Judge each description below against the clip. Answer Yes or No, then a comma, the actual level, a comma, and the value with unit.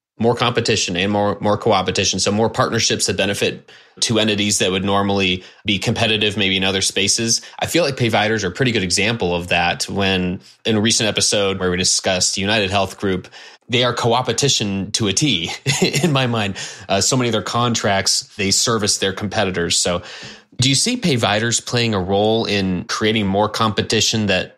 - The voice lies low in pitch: Yes, low, 105 Hz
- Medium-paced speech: Yes, average, 185 wpm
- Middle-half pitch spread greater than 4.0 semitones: No, average, 3.1 semitones